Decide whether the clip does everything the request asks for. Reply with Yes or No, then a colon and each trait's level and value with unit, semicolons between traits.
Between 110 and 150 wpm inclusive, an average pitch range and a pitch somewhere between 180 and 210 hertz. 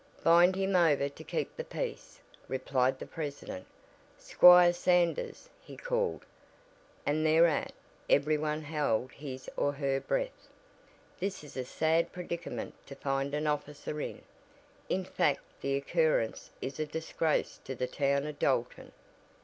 No: average, 140 wpm; average, 3.5 semitones; medium, 150 Hz